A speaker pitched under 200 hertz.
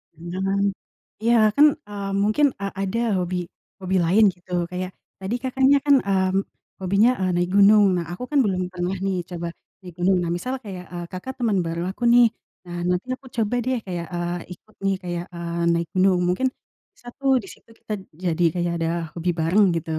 Yes: medium, 185 Hz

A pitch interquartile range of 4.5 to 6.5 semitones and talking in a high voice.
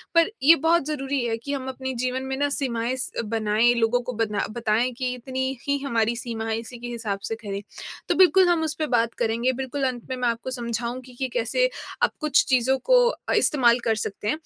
No: average, 2.7 semitones; very high, 250 Hz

